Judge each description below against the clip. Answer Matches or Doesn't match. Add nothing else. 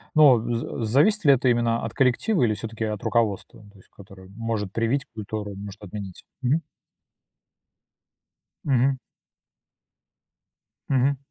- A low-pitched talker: Matches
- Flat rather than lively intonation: Doesn't match